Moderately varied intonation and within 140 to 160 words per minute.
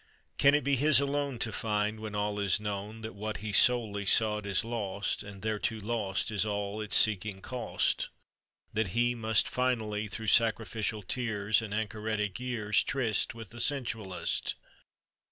No: narrow, 2.1 semitones; average, 155 wpm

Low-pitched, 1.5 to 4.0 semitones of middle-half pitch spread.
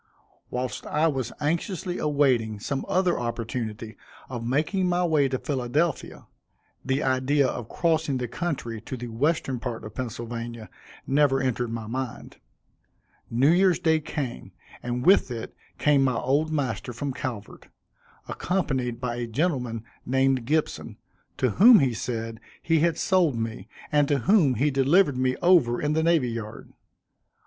No: low, 130 Hz; average, 4.5 semitones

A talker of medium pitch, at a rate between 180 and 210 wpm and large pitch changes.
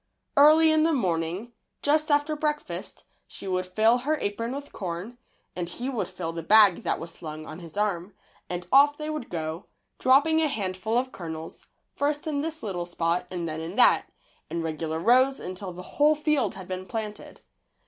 No: high, 210 Hz; average, 185 wpm; wide, 8.6 semitones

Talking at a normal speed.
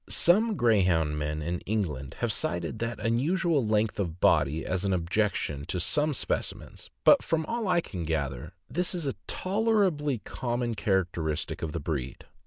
Yes: average, 165 wpm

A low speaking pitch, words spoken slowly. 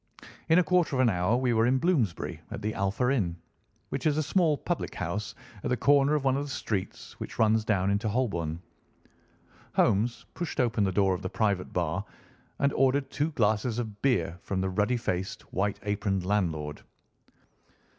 No: low, 110 Hz; average, 185 wpm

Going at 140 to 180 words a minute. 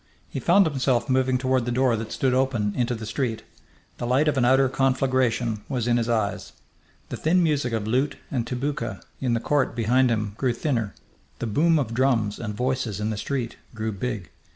No: average, 200 wpm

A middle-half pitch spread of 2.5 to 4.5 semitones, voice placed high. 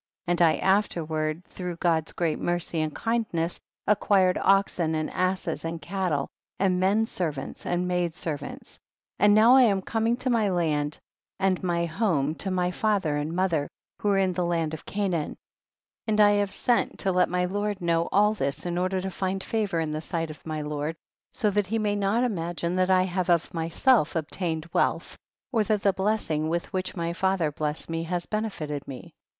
No: average, 3.5 semitones; medium, 180 Hz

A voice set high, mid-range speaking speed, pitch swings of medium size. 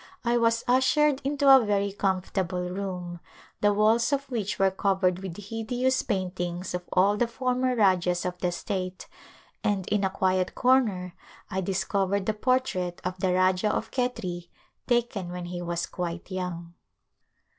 Yes: high, 195 Hz; average, 155 wpm; average, 4.2 semitones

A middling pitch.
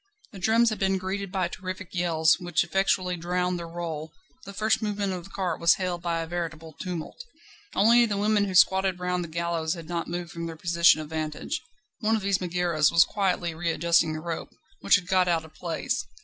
Yes: medium, 175 Hz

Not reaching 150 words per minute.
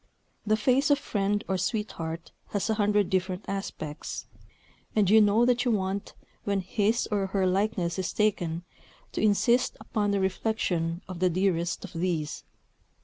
No: average, 155 wpm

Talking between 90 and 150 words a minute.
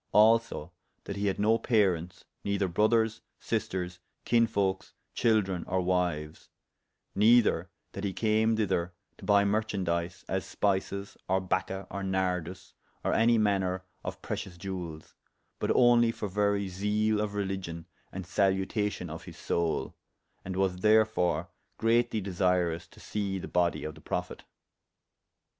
Yes: slow, 135 wpm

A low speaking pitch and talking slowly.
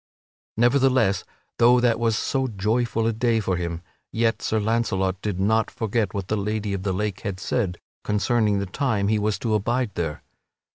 No: low, 110 Hz; average, 180 wpm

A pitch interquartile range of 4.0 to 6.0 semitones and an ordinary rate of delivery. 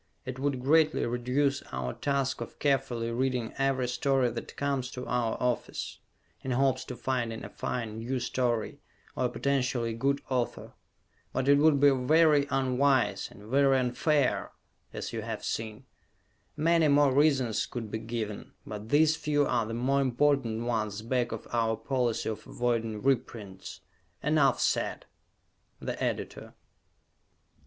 No: average, 3.0 semitones; average, 145 wpm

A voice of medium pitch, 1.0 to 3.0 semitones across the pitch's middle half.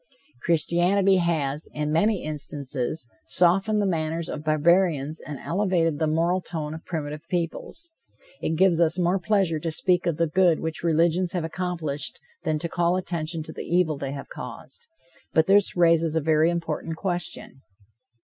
Yes: medium, 165 Hz; narrow, 2.5 semitones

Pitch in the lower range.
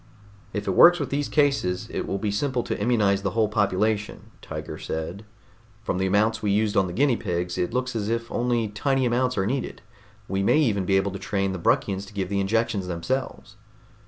Yes: low, 105 Hz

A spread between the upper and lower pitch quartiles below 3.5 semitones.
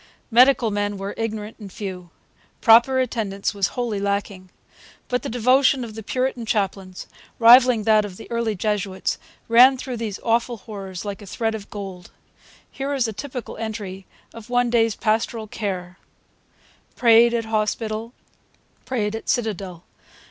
Yes: average, 2.9 semitones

